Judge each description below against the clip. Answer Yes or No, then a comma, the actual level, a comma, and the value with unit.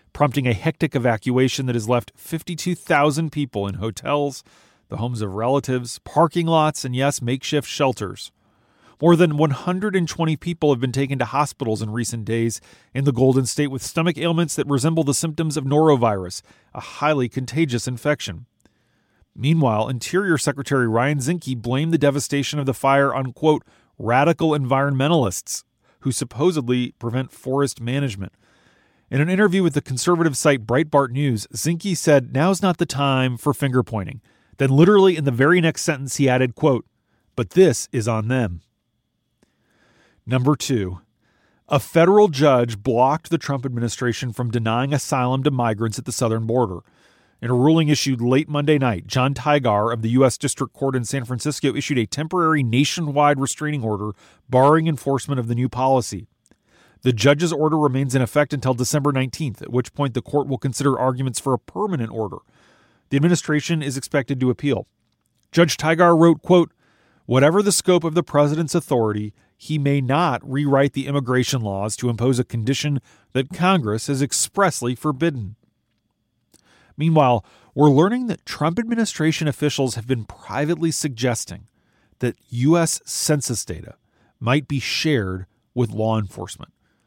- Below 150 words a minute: No, average, 155 wpm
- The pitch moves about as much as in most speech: Yes, average, 4.0 semitones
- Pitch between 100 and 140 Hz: Yes, low, 135 Hz